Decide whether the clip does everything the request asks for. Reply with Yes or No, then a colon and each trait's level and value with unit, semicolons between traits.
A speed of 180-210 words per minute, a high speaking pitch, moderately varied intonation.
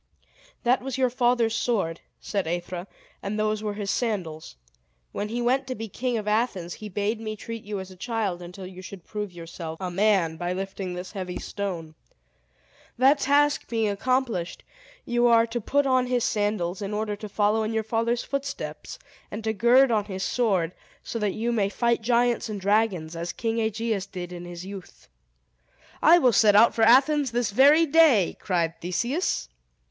Yes: average, 185 wpm; high, 215 Hz; average, 4.2 semitones